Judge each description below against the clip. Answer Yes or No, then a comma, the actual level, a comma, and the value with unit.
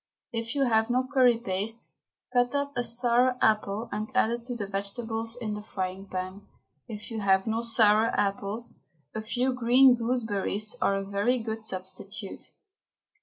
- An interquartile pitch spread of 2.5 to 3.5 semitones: Yes, average, 3.1 semitones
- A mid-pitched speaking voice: No, high, 225 Hz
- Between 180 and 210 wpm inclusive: No, average, 165 wpm